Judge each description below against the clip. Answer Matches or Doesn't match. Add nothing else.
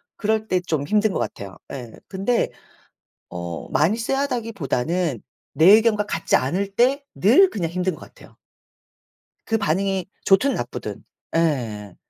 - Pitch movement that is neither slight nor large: Doesn't match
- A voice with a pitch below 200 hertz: Matches